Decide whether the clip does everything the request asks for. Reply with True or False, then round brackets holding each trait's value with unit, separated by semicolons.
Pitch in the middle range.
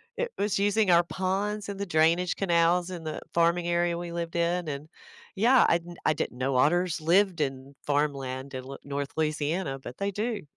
True (170 Hz)